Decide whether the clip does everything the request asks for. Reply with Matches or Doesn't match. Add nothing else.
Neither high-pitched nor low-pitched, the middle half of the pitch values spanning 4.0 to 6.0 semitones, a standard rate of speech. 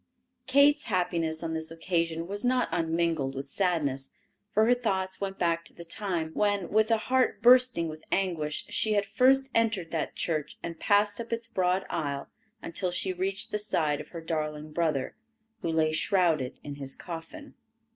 Matches